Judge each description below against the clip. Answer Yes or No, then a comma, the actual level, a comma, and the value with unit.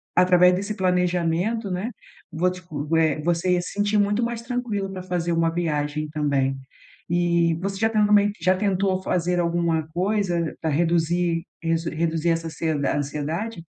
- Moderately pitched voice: Yes, medium, 175 Hz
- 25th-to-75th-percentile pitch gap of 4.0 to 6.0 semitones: No, average, 2.9 semitones